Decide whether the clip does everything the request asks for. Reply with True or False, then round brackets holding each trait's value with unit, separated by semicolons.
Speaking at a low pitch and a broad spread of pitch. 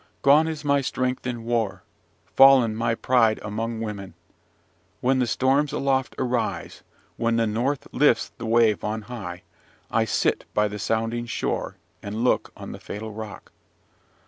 False (115 Hz; 3.0 semitones)